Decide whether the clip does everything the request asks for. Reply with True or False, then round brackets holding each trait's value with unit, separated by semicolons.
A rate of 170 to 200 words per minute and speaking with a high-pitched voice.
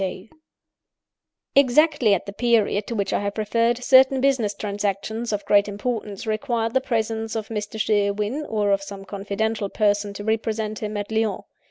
False (160 wpm; 215 Hz)